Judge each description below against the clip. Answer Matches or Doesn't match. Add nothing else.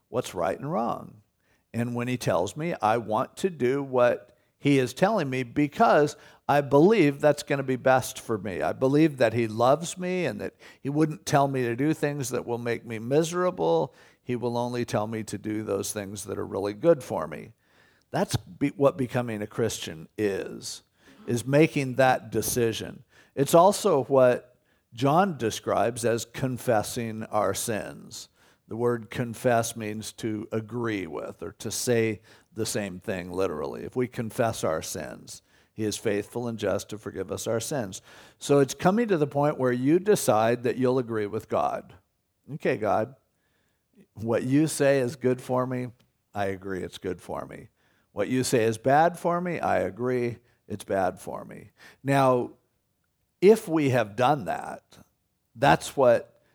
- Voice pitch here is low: Matches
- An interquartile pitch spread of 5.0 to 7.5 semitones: Doesn't match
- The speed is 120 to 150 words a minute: Doesn't match